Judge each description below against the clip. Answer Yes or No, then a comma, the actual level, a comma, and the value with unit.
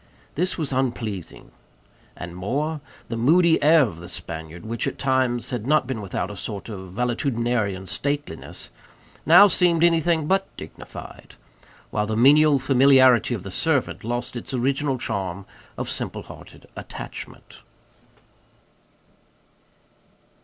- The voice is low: Yes, low, 125 Hz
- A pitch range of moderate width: No, wide, 5.8 semitones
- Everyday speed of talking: No, slow, 125 wpm